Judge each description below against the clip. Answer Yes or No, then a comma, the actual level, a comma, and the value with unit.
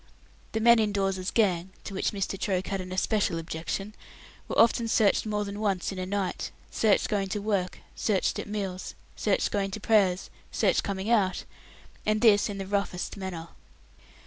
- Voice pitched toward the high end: Yes, high, 200 Hz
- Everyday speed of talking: Yes, average, 175 wpm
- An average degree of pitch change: No, narrow, 2.1 semitones